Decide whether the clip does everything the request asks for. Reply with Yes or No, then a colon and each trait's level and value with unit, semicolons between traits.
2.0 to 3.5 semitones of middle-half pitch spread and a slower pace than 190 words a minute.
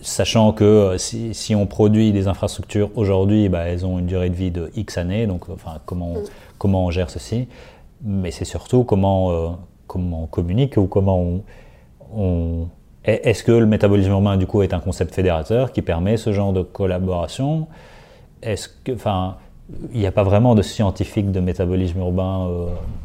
Yes: average, 2.8 semitones; average, 180 wpm